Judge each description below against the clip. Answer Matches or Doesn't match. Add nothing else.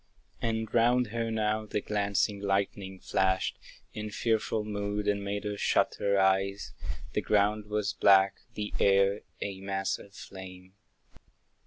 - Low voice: Matches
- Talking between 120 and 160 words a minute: Matches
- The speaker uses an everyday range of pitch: Doesn't match